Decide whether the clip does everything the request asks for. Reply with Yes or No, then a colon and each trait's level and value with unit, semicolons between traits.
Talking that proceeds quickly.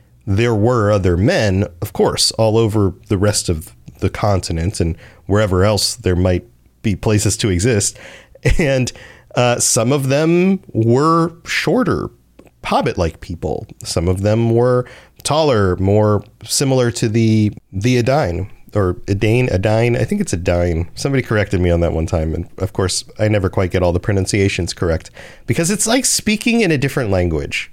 No: average, 160 wpm